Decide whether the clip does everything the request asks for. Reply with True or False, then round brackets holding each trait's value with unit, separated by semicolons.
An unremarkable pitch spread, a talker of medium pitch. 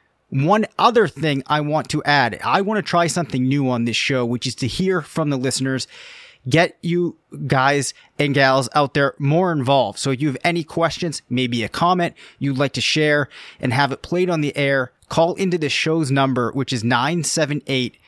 True (4.0 semitones; 145 Hz)